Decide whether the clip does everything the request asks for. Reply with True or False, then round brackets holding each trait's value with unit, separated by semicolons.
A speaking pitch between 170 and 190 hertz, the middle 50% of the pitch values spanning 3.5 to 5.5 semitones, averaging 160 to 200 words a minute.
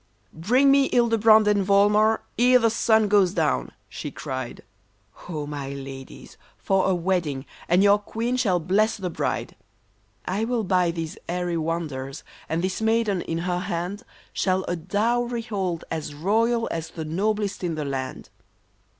True (185 Hz; 5.1 semitones; 165 wpm)